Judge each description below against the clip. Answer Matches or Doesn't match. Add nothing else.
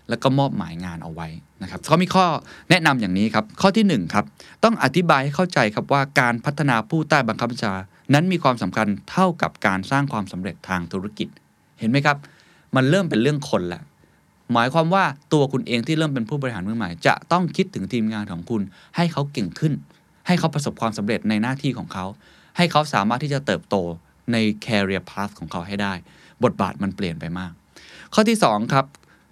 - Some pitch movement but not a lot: Doesn't match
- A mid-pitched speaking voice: Doesn't match